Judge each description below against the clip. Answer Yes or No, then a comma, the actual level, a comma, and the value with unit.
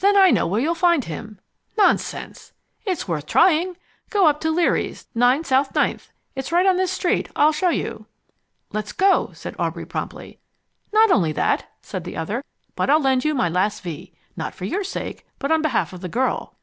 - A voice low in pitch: No, very high, 290 Hz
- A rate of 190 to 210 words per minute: Yes, average, 195 wpm